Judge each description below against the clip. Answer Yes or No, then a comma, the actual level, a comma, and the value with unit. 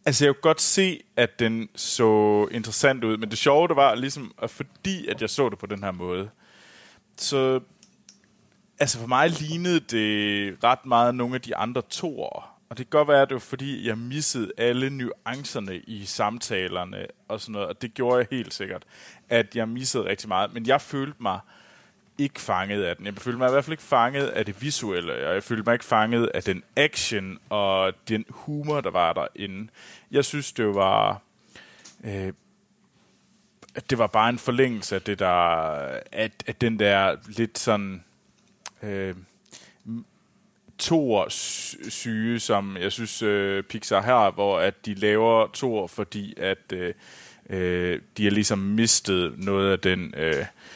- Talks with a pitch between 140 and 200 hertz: No, low, 115 Hz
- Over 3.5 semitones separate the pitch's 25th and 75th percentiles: Yes, average, 4.3 semitones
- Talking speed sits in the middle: Yes, average, 175 wpm